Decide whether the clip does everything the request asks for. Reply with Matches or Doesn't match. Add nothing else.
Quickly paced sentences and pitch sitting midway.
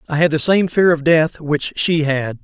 Matches